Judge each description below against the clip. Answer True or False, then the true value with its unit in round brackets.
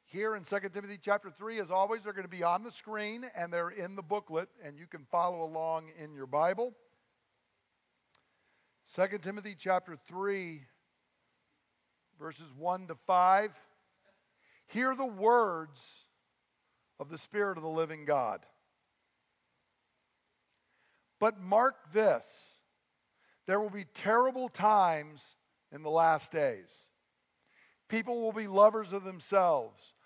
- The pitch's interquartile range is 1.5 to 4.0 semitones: False (4.6 semitones)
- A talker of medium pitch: False (195 Hz)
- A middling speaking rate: False (130 wpm)